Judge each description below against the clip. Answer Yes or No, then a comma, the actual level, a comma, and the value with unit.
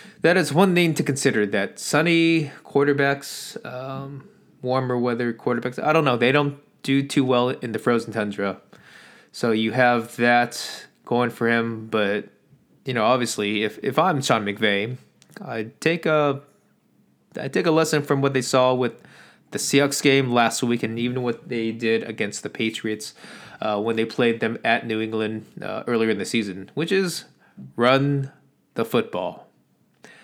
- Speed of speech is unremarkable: Yes, average, 165 wpm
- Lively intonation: No, average, 4.0 semitones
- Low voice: Yes, low, 125 Hz